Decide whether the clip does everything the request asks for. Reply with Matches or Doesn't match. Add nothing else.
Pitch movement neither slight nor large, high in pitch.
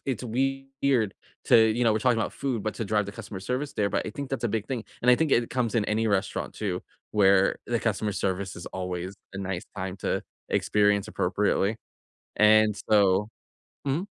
Doesn't match